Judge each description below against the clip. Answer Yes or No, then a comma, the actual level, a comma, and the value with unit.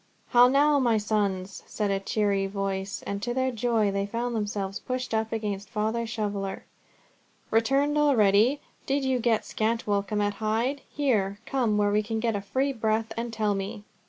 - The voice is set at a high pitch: Yes, high, 220 Hz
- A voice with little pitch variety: No, average, 3.0 semitones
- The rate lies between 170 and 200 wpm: Yes, average, 180 wpm